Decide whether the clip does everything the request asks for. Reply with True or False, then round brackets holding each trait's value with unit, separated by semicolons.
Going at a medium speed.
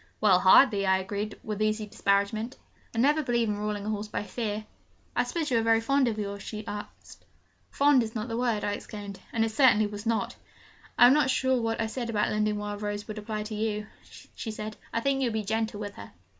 False (235 wpm)